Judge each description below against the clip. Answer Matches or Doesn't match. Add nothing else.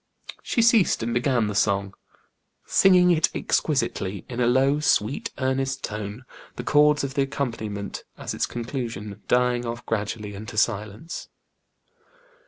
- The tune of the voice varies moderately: Matches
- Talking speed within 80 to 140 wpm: Matches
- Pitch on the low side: Matches